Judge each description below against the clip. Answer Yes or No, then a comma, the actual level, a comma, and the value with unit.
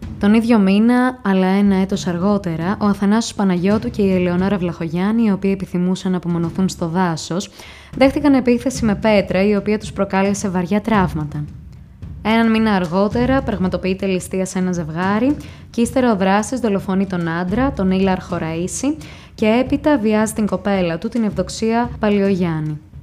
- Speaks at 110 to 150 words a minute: Yes, average, 145 wpm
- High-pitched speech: Yes, high, 195 Hz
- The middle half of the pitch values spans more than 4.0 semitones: No, average, 3.3 semitones